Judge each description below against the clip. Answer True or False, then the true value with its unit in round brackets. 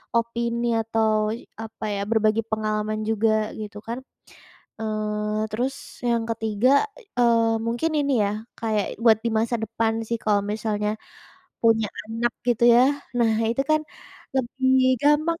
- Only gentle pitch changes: True (1.7 semitones)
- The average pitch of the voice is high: True (225 Hz)